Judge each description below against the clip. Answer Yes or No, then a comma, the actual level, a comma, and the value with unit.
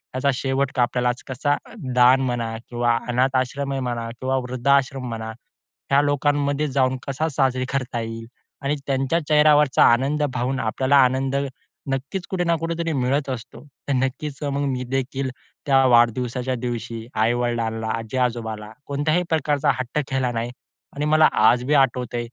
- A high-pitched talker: No, low, 130 Hz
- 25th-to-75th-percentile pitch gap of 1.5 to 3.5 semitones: Yes, average, 2.7 semitones